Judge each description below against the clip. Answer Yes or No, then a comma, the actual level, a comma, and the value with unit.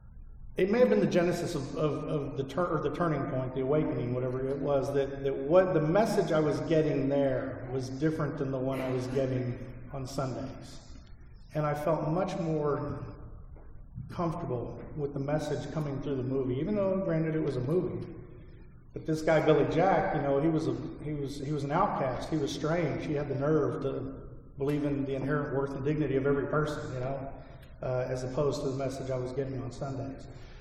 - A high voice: No, medium, 140 Hz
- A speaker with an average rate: No, fast, 210 wpm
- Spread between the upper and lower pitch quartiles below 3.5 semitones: Yes, narrow, 2.6 semitones